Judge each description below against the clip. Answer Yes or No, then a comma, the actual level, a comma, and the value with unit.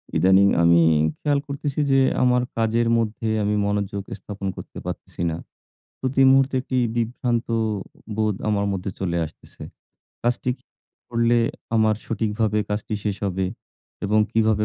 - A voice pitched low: Yes, low, 110 Hz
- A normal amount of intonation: Yes, average, 3.0 semitones